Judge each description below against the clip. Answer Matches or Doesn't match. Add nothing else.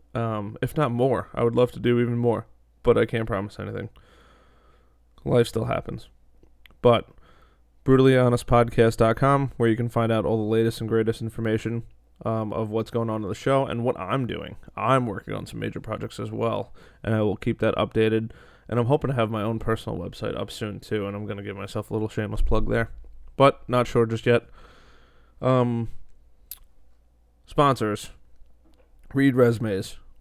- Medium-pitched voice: Doesn't match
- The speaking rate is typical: Matches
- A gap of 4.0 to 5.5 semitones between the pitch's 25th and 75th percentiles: Doesn't match